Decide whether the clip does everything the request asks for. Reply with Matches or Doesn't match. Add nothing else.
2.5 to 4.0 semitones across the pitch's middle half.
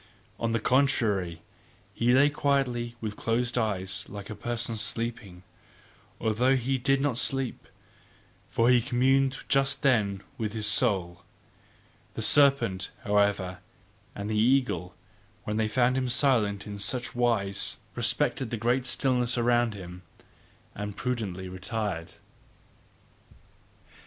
Matches